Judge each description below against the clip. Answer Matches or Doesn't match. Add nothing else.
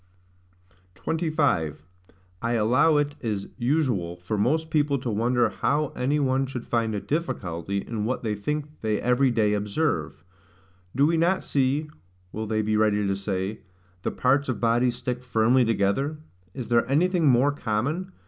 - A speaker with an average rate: Matches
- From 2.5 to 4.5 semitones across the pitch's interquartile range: Doesn't match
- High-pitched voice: Doesn't match